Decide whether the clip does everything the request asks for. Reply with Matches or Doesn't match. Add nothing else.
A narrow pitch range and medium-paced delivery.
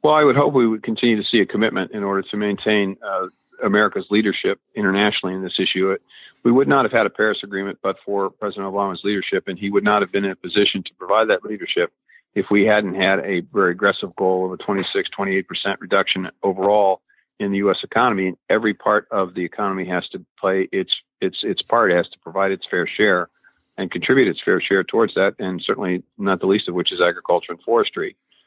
Doesn't match